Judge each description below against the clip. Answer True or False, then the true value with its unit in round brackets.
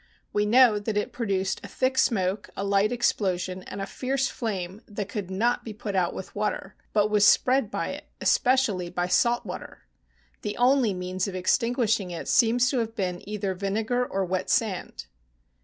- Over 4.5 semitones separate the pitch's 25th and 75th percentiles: False (3.9 semitones)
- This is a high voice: True (210 Hz)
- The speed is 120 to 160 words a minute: False (185 wpm)